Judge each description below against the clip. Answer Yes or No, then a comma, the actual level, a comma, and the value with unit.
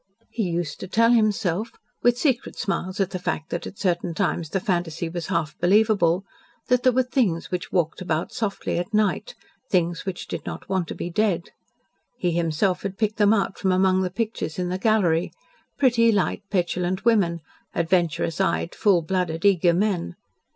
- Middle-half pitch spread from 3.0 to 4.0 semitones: Yes, average, 3.7 semitones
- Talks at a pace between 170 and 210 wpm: Yes, average, 180 wpm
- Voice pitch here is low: No, medium, 185 Hz